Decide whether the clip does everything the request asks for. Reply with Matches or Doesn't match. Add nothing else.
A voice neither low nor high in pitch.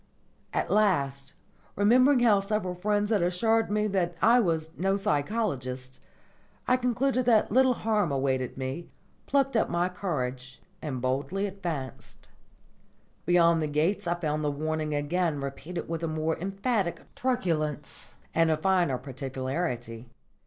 Matches